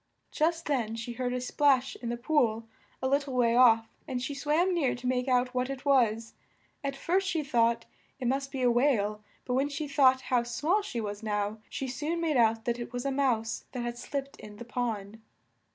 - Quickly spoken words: Yes, fast, 215 wpm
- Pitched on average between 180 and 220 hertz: No, very high, 250 Hz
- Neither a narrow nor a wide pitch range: Yes, average, 3.1 semitones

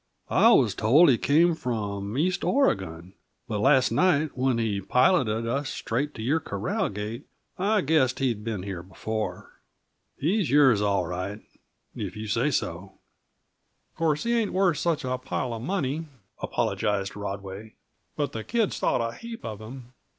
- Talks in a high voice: No, low, 125 Hz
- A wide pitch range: Yes, wide, 6.5 semitones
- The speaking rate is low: No, average, 160 wpm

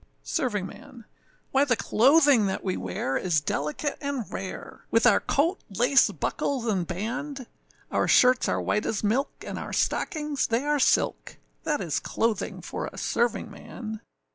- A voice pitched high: Yes, high, 235 Hz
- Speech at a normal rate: Yes, average, 150 wpm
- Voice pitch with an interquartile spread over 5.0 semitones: Yes, wide, 5.6 semitones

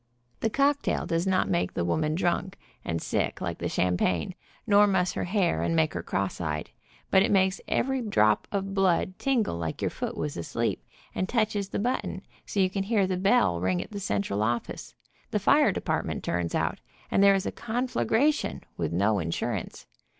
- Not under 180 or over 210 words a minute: Yes, average, 185 wpm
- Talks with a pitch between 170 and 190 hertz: Yes, medium, 185 Hz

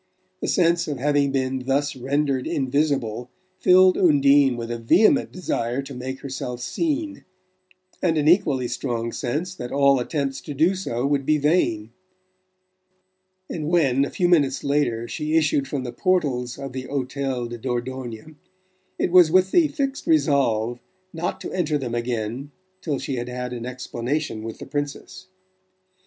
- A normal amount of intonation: Yes, average, 4.0 semitones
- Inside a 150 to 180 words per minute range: Yes, average, 155 wpm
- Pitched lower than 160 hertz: Yes, medium, 140 Hz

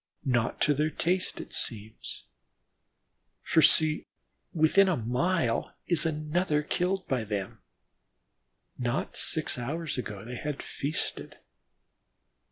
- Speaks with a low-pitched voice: No, medium, 150 Hz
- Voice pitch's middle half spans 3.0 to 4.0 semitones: No, wide, 5.5 semitones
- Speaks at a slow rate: Yes, slow, 110 wpm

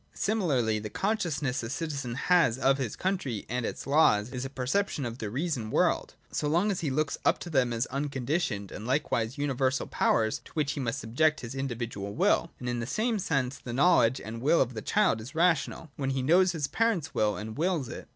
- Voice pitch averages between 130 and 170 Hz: Yes, low, 135 Hz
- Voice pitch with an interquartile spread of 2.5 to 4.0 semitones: No, average, 5.3 semitones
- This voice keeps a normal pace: No, fast, 215 wpm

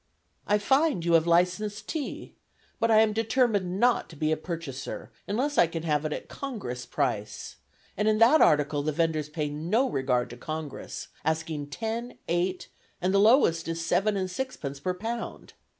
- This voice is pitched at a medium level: Yes, medium, 175 Hz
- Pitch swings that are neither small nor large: No, wide, 6.2 semitones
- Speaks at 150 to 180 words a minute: Yes, average, 175 wpm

